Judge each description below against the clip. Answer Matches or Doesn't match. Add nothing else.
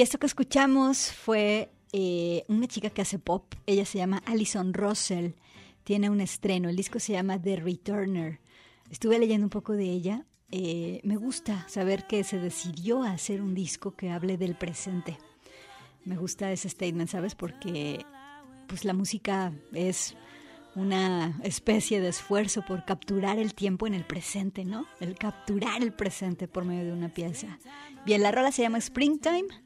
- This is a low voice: Doesn't match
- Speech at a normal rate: Matches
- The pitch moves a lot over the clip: Doesn't match